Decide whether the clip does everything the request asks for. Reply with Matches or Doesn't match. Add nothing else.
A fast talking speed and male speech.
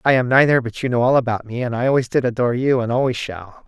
Matches